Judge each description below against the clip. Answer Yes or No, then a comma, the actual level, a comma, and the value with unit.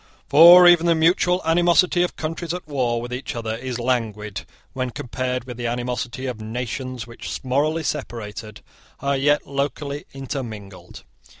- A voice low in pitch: Yes, low, 130 Hz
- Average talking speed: Yes, average, 145 wpm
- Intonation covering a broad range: No, average, 4.6 semitones